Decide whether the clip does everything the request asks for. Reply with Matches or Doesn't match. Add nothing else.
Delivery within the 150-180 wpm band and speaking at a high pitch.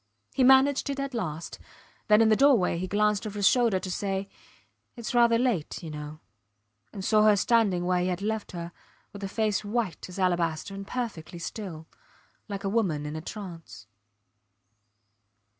Matches